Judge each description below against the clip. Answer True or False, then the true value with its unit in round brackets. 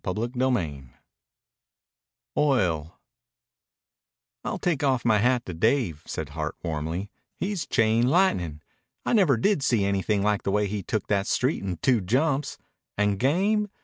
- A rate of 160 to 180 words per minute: False (145 wpm)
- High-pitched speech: False (110 Hz)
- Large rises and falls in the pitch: True (6.0 semitones)